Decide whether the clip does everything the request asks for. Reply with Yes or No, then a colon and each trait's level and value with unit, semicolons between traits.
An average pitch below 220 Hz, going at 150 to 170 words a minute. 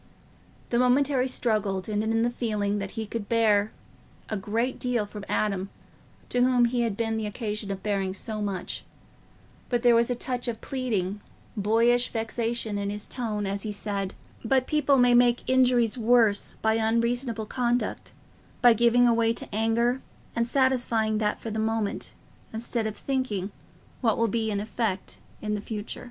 No: high, 225 Hz; average, 165 wpm